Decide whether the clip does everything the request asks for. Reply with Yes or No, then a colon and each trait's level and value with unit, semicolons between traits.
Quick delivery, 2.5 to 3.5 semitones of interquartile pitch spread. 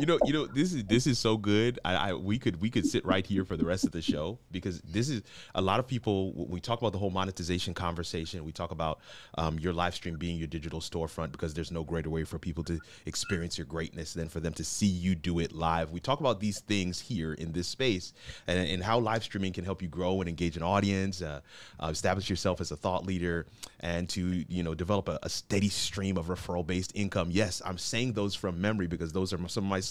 Yes: fast, 250 wpm; average, 2.9 semitones